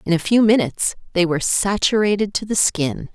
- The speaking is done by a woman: Yes, female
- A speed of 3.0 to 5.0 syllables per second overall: No, 5.6 syllables/s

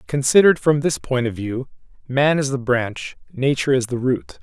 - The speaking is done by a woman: No, male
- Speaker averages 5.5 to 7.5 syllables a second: No, 5.1 syllables/s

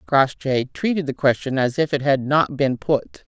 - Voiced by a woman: Yes, female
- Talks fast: No, average, 195 wpm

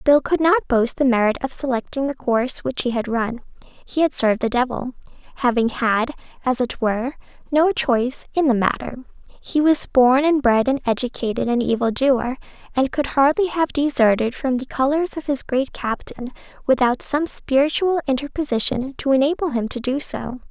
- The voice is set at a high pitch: Yes, very high, 260 Hz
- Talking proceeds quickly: No, average, 180 wpm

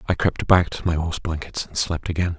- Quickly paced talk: Yes, fast, 250 wpm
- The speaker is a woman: No, male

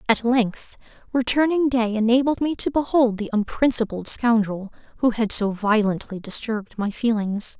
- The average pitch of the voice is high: Yes, high, 230 Hz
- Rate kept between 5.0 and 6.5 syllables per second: No, 4.7 syllables/s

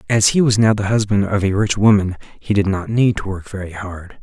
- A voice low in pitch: Yes, low, 100 Hz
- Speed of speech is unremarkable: No, fast, 255 wpm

